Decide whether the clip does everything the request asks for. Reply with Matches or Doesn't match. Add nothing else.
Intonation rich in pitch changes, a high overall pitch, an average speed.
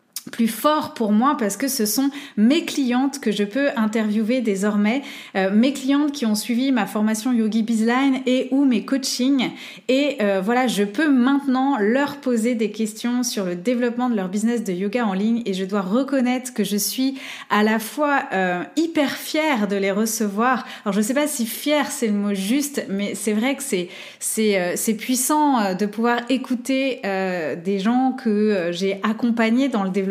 Doesn't match